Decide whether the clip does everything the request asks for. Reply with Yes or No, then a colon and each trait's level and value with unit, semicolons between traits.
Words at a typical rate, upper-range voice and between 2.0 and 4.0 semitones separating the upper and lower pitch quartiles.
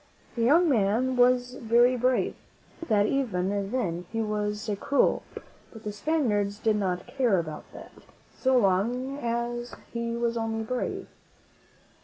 Yes: average, 145 wpm; high, 230 Hz; average, 3.4 semitones